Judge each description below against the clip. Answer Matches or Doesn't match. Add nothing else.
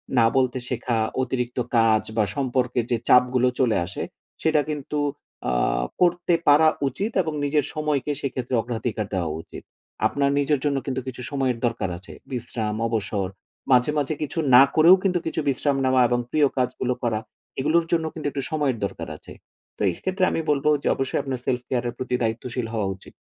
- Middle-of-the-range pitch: Doesn't match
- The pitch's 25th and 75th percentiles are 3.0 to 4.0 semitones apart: Matches